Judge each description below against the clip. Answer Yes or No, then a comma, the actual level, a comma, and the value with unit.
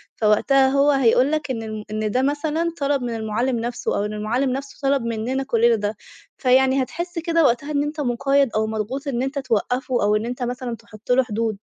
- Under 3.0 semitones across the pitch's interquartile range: No, average, 3.7 semitones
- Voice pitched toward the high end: Yes, very high, 250 Hz